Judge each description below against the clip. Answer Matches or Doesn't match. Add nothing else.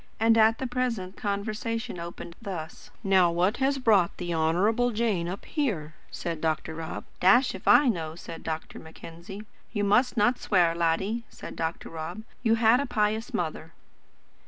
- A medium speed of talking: Matches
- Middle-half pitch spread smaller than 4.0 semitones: Doesn't match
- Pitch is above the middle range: Matches